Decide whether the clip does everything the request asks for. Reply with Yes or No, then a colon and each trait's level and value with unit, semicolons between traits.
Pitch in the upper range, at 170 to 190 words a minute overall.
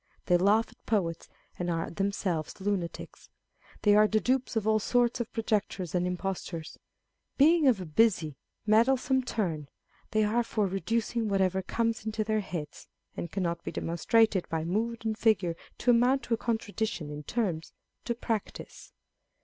No: high, 210 Hz; average, 160 wpm